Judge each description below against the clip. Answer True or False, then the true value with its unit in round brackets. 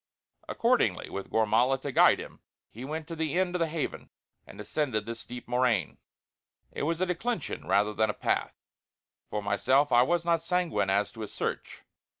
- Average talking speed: True (180 wpm)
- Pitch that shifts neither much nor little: False (7.2 semitones)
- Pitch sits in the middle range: False (130 Hz)